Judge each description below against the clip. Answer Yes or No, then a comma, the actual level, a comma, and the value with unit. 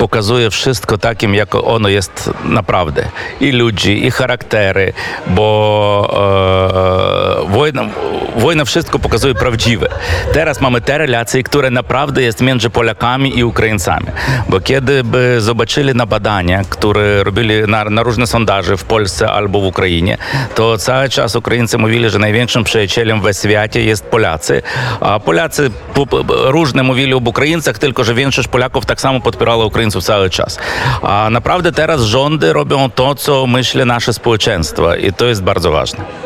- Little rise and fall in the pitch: No, average, 3.7 semitones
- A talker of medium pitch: No, low, 120 Hz